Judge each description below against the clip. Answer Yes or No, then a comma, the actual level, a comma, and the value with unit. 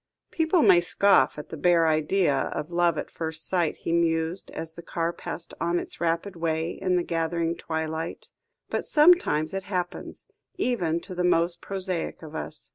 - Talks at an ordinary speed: Yes, average, 175 wpm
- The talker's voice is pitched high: No, medium, 170 Hz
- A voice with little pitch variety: Yes, narrow, 2.0 semitones